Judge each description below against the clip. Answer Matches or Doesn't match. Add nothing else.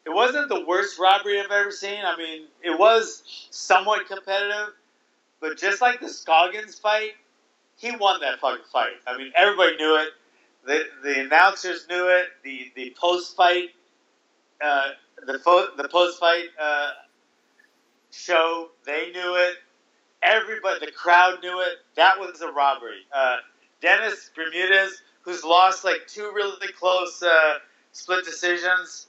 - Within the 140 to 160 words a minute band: Matches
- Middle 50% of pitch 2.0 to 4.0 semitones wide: Matches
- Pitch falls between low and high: Matches